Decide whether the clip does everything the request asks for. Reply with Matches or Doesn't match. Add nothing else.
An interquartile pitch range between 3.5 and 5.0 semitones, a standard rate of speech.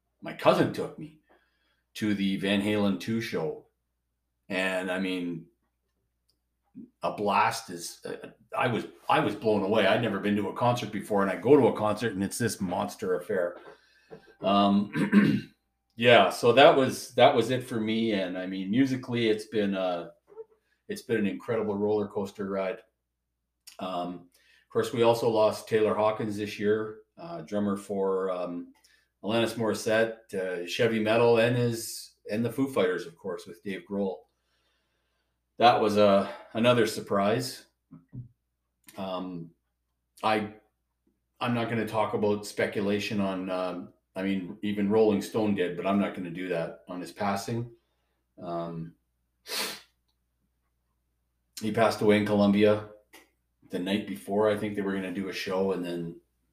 Matches